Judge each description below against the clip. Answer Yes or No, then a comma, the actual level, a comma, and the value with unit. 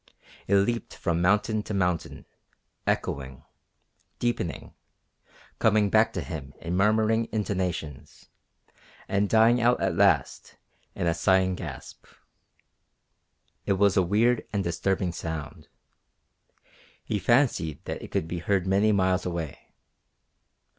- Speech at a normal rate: No, slow, 120 wpm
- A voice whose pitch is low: Yes, very low, 95 Hz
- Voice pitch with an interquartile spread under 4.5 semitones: Yes, average, 4.0 semitones